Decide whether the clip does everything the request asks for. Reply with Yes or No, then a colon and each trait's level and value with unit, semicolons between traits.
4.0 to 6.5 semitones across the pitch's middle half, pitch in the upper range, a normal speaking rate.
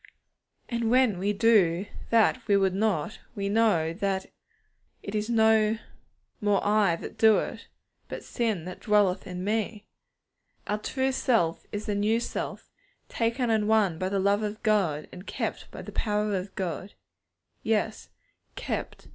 No: narrow, 2.5 semitones; high, 210 Hz; average, 155 wpm